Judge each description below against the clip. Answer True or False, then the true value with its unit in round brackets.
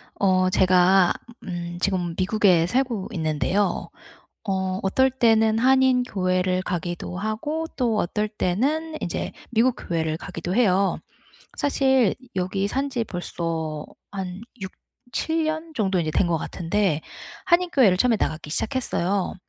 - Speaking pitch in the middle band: False (195 Hz)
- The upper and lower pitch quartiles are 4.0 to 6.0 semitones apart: True (5.6 semitones)